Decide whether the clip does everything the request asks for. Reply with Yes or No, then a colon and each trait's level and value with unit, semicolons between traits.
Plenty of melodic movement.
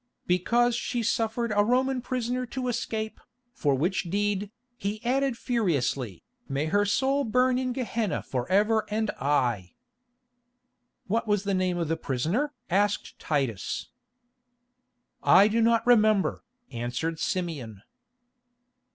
Yes: wide, 6.5 semitones